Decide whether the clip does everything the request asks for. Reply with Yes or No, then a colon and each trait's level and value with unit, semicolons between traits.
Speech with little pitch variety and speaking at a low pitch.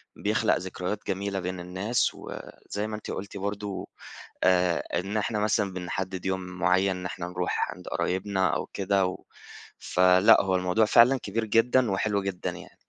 Yes: narrow, 2.1 semitones; very low, 95 Hz